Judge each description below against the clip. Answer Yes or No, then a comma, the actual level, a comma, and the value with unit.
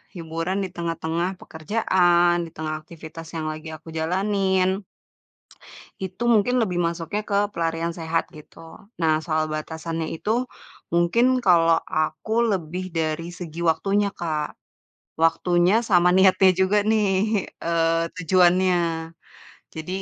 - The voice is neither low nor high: Yes, medium, 170 Hz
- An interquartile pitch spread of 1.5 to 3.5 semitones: Yes, narrow, 2.5 semitones